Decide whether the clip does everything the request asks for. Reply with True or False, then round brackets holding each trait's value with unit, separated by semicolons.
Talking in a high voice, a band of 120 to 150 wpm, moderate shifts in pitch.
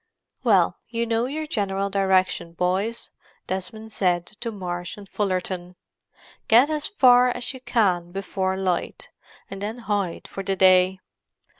True (195 Hz; 140 wpm; 3.8 semitones)